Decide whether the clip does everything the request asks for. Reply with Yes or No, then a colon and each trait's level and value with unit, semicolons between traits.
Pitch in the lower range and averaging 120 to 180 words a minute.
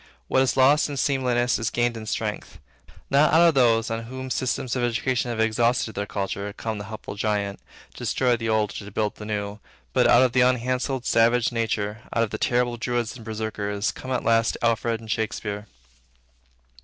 No: low, 115 Hz; average, 190 wpm